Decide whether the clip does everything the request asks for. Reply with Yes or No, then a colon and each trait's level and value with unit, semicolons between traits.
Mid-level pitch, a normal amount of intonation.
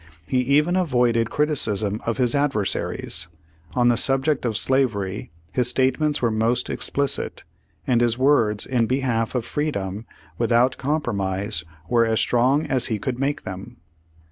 No: low, 120 Hz; average, 3.4 semitones